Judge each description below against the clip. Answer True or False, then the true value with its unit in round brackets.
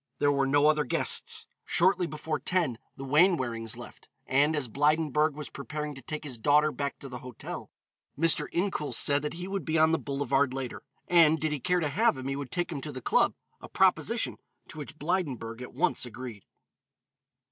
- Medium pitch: True (150 Hz)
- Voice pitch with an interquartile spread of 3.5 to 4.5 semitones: False (2.9 semitones)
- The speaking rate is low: False (195 wpm)